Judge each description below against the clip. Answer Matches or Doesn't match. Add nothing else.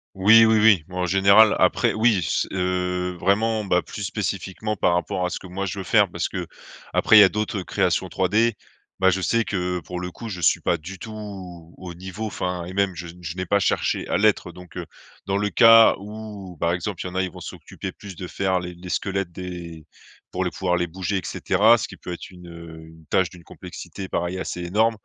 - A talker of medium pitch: Doesn't match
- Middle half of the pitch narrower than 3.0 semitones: Matches